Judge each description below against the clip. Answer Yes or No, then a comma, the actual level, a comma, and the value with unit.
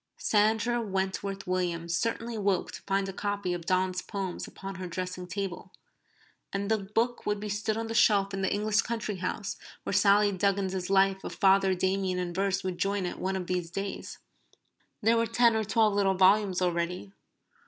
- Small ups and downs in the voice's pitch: Yes, narrow, 2.0 semitones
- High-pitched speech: Yes, high, 195 Hz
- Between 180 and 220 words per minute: Yes, average, 185 wpm